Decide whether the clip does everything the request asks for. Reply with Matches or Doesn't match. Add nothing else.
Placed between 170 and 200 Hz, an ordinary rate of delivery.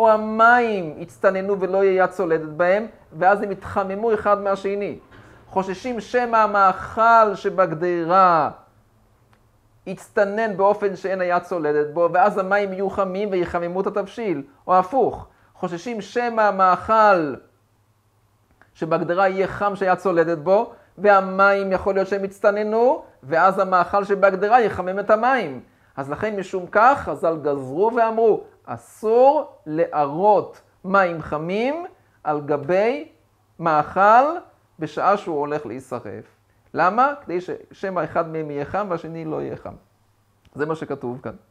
Matches